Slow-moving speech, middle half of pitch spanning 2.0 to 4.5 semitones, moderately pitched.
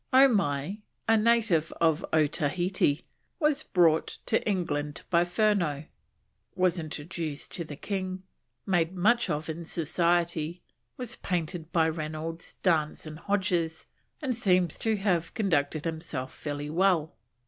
Yes: slow, 125 wpm; average, 3.6 semitones; medium, 170 Hz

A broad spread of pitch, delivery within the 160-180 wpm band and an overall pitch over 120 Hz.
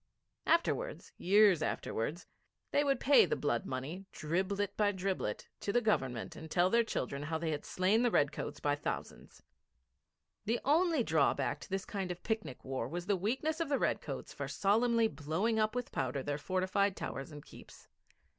Yes: wide, 6.9 semitones; average, 175 wpm; high, 190 Hz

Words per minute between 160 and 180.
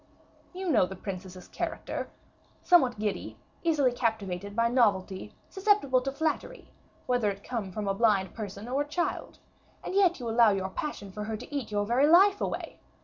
Yes: average, 175 wpm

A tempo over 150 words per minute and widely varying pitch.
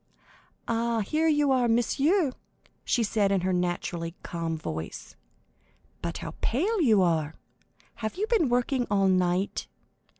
No: slow, 135 wpm; wide, 7.2 semitones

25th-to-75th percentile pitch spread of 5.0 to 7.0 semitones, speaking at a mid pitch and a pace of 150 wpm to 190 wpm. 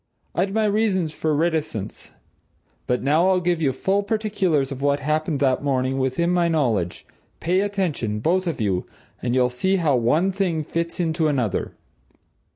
Yes: wide, 5.6 semitones; medium, 155 Hz; average, 160 wpm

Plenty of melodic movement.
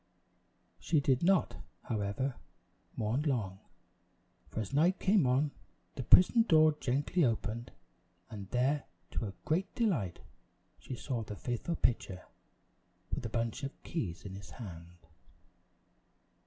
Yes: wide, 6.3 semitones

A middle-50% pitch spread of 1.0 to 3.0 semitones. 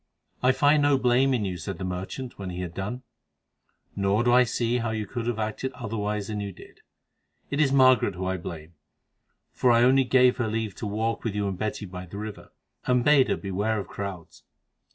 No: average, 4.3 semitones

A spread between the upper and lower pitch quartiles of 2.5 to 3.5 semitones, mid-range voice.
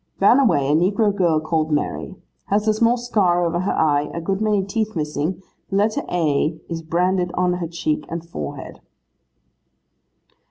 No: average, 4.2 semitones; medium, 175 Hz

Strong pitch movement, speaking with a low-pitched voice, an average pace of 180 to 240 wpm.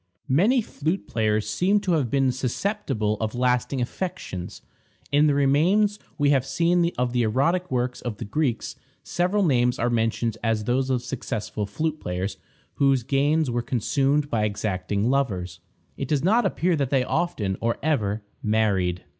No: wide, 5.7 semitones; low, 125 Hz; average, 155 wpm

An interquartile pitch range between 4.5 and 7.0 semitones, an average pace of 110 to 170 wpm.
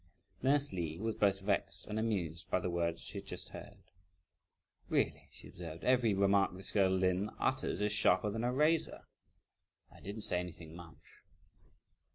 No: average, 3.7 semitones; average, 165 wpm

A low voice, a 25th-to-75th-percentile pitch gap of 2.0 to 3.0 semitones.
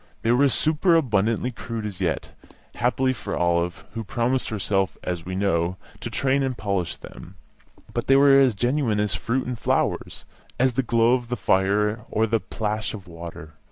No: low, 115 Hz; average, 4.7 semitones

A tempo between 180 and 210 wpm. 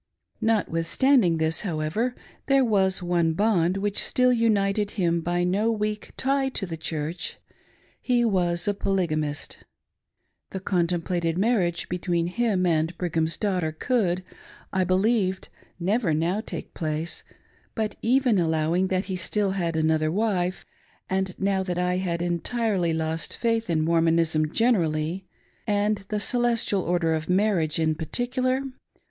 No: average, 140 wpm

